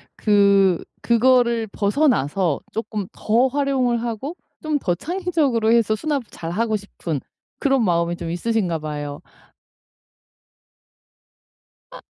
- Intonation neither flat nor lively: No, wide, 6.4 semitones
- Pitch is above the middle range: Yes, high, 220 Hz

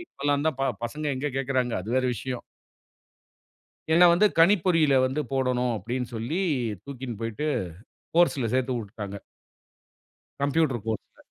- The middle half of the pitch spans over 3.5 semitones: Yes, average, 4.2 semitones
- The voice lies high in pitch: No, low, 130 Hz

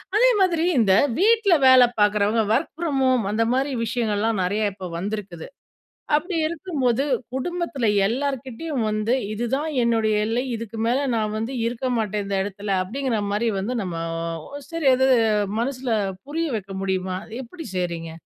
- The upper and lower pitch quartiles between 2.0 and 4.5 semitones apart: No, average, 4.9 semitones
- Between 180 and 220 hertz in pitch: No, high, 230 Hz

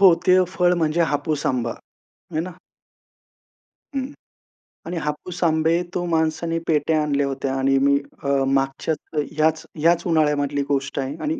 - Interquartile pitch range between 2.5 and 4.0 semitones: Yes, average, 3.0 semitones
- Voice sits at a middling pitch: Yes, medium, 155 Hz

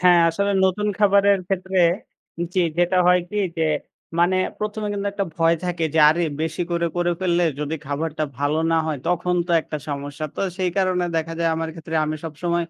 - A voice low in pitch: No, medium, 175 Hz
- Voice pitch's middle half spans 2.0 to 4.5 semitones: Yes, narrow, 2.6 semitones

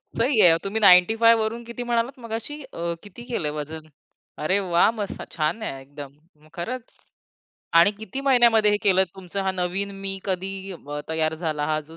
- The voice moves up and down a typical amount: No, wide, 5.8 semitones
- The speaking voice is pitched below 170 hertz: No, high, 195 Hz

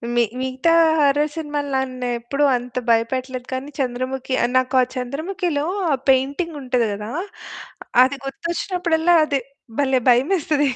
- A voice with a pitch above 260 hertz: Yes, very high, 270 Hz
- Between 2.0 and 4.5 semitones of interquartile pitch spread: Yes, average, 2.9 semitones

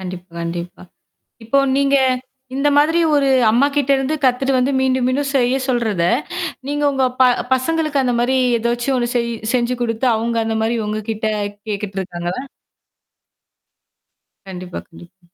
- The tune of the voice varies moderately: Yes, average, 4.4 semitones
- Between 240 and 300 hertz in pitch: Yes, high, 245 Hz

